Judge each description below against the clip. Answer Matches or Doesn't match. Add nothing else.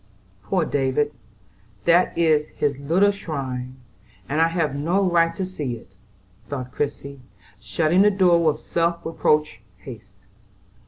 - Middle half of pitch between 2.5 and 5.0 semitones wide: Matches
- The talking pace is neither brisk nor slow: Doesn't match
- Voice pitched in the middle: Matches